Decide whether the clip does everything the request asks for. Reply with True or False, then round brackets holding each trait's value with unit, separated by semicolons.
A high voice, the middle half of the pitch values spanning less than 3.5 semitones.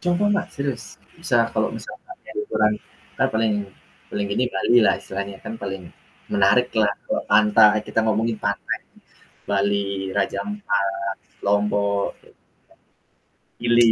False (105 Hz; 2.9 semitones)